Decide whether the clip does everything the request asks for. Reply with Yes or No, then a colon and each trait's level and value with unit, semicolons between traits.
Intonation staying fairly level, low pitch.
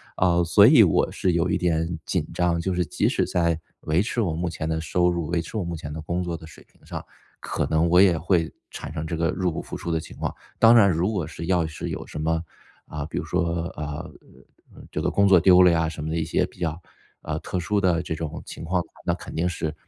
Yes: narrow, 1.9 semitones; very low, 85 Hz